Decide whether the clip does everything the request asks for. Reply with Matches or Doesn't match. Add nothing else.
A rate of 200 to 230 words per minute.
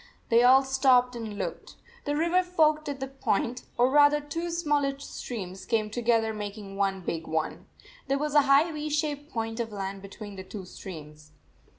Doesn't match